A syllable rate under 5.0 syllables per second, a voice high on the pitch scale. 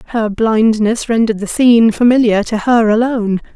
No: 5.4 syllables/s; high, 225 Hz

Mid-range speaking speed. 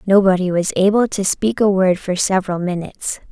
Yes: average, 180 wpm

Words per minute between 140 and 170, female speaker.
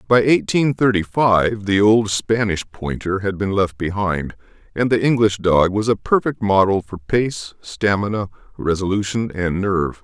No: average, 155 wpm; male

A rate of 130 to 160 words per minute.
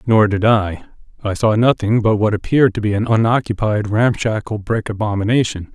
Yes: average, 155 wpm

